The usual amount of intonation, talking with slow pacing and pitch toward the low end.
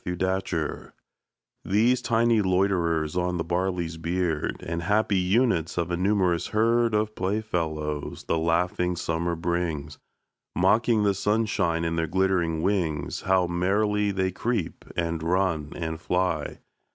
Yes: average, 3.5 semitones; slow, 125 wpm; very low, 90 Hz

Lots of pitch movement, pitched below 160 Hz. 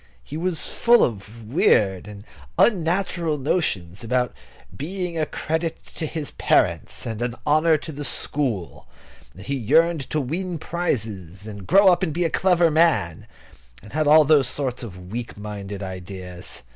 Yes: wide, 8.0 semitones; medium, 140 Hz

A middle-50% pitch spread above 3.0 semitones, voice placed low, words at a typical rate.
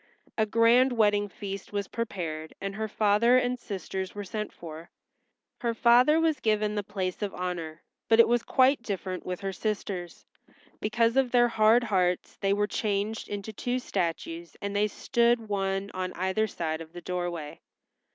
No: average, 3.9 semitones; high, 205 Hz; average, 170 wpm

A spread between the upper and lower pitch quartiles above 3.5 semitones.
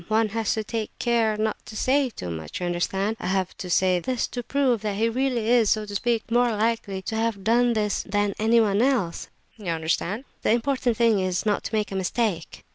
No: average, 3.1 semitones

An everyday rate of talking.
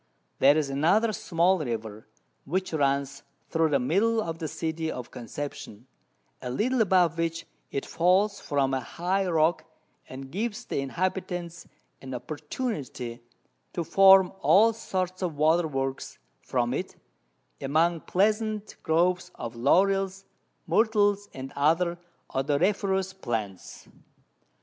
No: slow, 120 wpm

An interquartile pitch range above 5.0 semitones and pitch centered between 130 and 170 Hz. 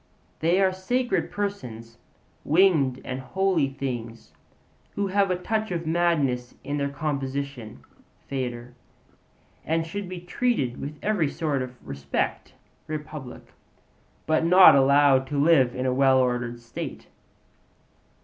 Yes: wide, 5.6 semitones; medium, 140 Hz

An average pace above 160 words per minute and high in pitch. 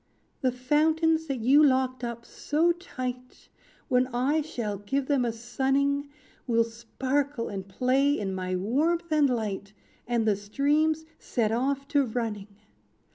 No: average, 140 wpm; very high, 255 Hz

